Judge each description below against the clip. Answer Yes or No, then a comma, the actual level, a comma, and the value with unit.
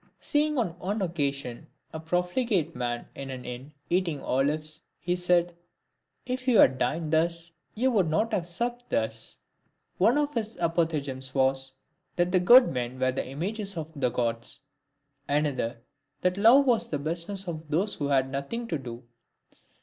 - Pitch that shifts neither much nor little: No, wide, 6.7 semitones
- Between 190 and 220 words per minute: No, average, 160 wpm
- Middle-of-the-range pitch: Yes, medium, 165 Hz